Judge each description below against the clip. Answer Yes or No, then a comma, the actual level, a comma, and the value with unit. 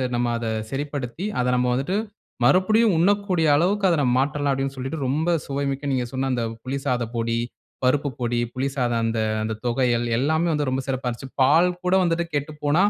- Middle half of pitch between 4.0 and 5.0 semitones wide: Yes, average, 4.5 semitones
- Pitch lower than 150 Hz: Yes, low, 135 Hz